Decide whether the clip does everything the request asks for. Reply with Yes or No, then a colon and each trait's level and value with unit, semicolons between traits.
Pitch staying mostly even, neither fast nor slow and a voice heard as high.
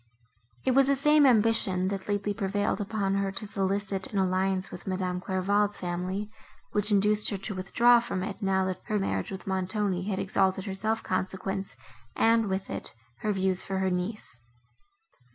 Yes: narrow, 1.8 semitones; average, 170 wpm; high, 195 Hz